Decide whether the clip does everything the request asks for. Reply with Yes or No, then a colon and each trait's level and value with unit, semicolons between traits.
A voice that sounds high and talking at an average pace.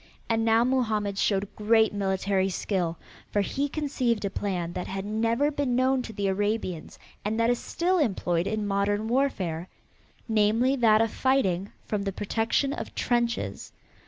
Yes: high, 215 Hz; average, 160 wpm